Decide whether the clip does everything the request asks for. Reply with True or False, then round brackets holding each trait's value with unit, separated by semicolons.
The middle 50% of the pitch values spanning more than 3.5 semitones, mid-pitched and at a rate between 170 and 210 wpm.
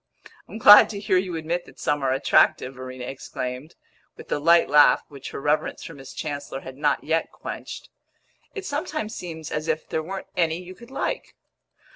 True (4.7 semitones; 160 Hz; 185 wpm)